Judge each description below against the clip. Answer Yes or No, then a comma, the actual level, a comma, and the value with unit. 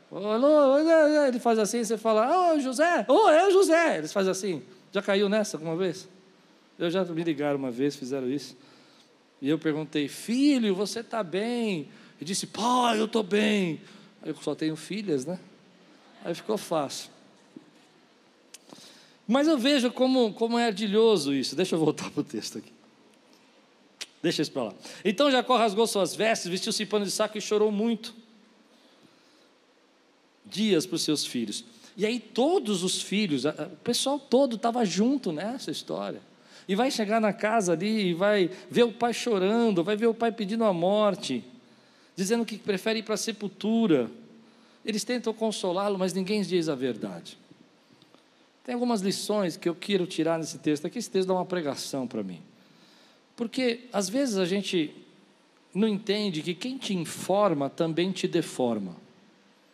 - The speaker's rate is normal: Yes, average, 165 wpm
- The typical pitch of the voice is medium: No, high, 210 Hz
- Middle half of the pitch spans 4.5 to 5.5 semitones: Yes, average, 4.8 semitones